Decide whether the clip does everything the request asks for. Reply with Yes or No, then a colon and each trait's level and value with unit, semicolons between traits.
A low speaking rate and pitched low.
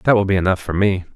No: fast, 310 wpm; very low, 95 Hz